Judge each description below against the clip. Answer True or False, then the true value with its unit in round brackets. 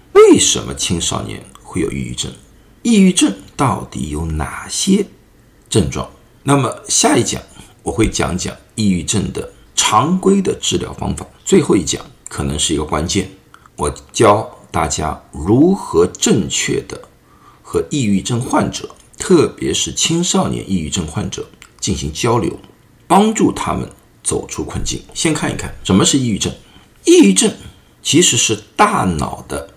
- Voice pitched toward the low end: True (120 Hz)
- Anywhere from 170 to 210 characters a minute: False (220 characters per minute)